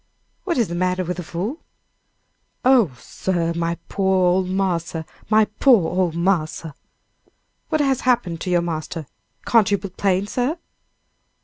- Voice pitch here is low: No, medium, 185 Hz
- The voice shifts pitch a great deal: No, average, 4.2 semitones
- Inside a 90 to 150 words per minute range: Yes, average, 145 wpm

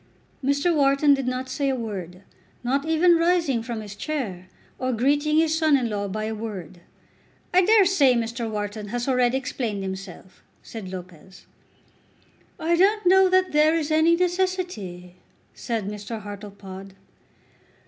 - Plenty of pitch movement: Yes, wide, 7.4 semitones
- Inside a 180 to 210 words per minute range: No, average, 150 wpm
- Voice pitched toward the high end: Yes, very high, 250 Hz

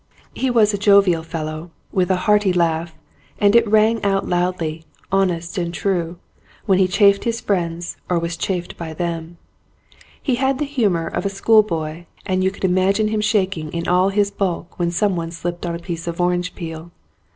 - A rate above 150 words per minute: Yes, average, 185 wpm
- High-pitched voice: No, medium, 180 Hz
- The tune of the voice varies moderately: Yes, average, 3.1 semitones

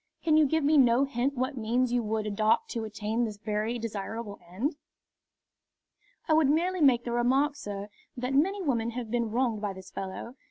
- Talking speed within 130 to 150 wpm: No, average, 190 wpm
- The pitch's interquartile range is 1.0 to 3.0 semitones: No, average, 4.1 semitones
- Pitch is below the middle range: No, high, 240 Hz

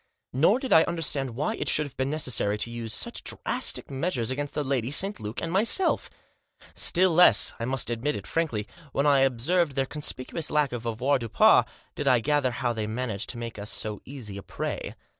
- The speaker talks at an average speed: No, fast, 215 wpm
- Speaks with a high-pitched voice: No, low, 135 Hz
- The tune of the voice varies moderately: Yes, average, 4.4 semitones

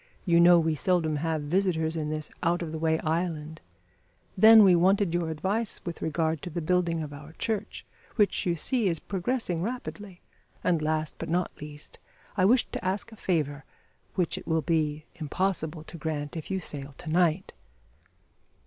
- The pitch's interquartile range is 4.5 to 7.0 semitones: No, average, 3.0 semitones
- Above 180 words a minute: No, average, 175 wpm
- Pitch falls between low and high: Yes, medium, 165 Hz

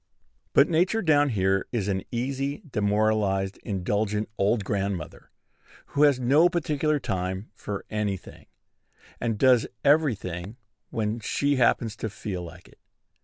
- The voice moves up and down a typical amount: No, wide, 6.1 semitones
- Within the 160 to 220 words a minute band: No, slow, 135 wpm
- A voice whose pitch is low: Yes, low, 110 Hz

